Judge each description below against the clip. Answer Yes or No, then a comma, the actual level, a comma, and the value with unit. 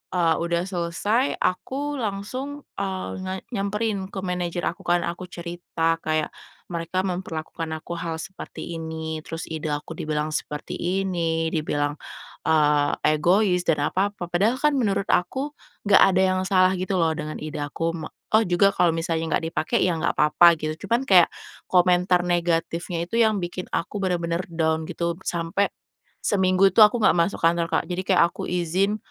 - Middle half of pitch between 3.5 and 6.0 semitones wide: No, average, 2.8 semitones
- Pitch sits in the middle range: Yes, medium, 175 Hz